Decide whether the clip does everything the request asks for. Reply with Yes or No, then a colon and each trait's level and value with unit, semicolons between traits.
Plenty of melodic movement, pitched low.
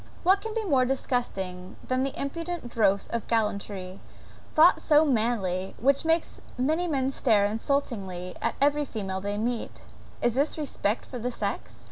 No: wide, 6.0 semitones; high, 245 Hz